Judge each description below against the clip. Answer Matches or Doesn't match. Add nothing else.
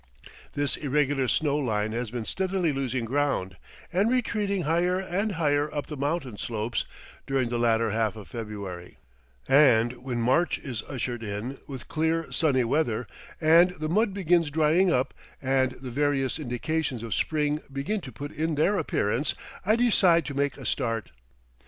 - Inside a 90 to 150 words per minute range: Doesn't match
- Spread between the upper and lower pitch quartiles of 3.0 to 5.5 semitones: Matches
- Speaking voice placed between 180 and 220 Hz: Doesn't match